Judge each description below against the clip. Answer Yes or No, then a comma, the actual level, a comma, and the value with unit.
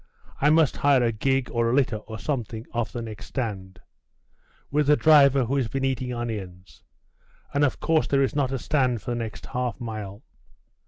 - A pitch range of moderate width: Yes, average, 3.7 semitones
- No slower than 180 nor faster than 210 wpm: Yes, average, 200 wpm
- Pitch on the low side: Yes, low, 125 Hz